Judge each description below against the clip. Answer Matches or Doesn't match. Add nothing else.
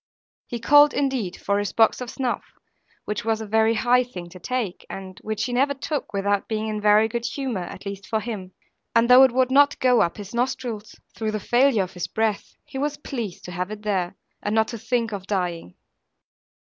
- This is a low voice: Doesn't match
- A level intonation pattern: Doesn't match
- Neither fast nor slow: Doesn't match